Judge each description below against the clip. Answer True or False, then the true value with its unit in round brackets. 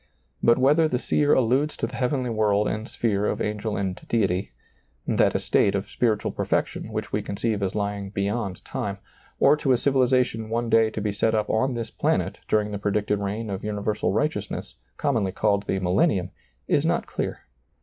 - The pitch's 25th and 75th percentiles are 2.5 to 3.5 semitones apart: True (2.8 semitones)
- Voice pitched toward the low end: True (105 Hz)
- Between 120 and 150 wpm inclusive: False (190 wpm)